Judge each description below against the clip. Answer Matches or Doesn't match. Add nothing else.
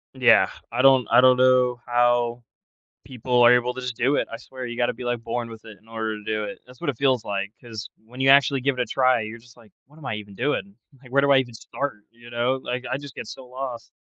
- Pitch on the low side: Matches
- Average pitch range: Doesn't match